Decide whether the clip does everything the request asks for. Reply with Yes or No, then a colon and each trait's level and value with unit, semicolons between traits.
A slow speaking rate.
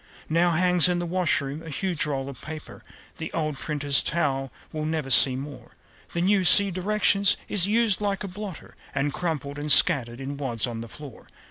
No: average, 190 wpm